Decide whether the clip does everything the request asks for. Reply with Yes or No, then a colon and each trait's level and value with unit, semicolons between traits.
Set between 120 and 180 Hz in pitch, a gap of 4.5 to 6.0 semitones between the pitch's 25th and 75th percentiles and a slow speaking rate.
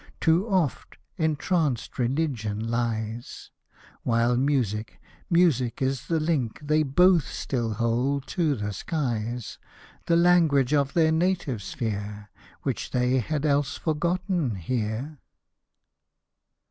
Yes: low, 135 Hz; wide, 5.4 semitones; slow, 110 wpm